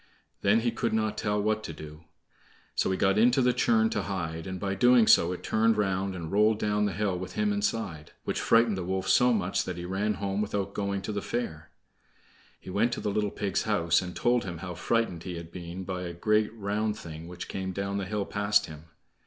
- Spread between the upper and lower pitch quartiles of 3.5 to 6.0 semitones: No, average, 2.9 semitones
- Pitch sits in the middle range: No, low, 100 Hz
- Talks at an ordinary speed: No, fast, 225 wpm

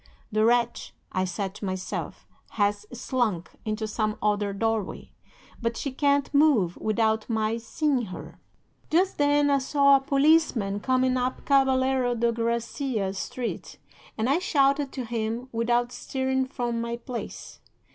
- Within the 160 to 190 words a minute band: No, average, 140 wpm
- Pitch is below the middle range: No, high, 240 Hz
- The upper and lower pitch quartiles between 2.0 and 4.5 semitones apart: Yes, average, 3.7 semitones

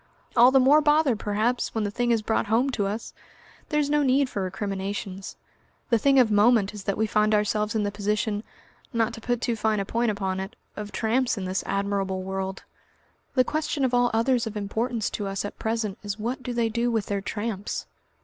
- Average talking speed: No, fast, 210 wpm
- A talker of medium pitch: No, high, 220 Hz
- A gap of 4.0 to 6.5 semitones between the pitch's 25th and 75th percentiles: No, average, 3.1 semitones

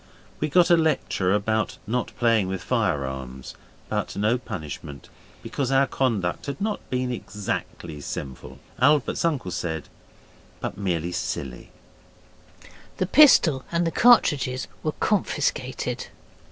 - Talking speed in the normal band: No, slow, 120 wpm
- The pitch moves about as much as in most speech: No, wide, 8.8 semitones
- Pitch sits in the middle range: No, low, 115 Hz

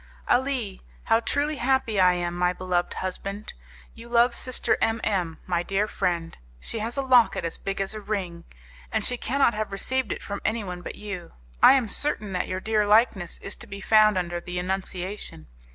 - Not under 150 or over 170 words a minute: No, average, 190 wpm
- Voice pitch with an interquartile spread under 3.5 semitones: No, average, 4.1 semitones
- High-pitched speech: Yes, high, 200 Hz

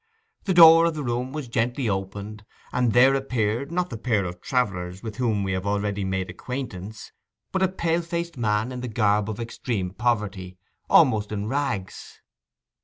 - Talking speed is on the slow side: No, average, 170 wpm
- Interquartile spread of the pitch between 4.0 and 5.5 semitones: Yes, average, 4.6 semitones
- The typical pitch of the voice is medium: No, low, 115 Hz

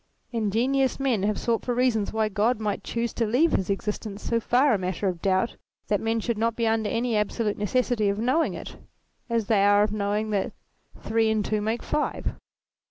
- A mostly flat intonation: Yes, narrow, 2.2 semitones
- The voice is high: Yes, high, 220 Hz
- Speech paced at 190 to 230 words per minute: Yes, average, 200 wpm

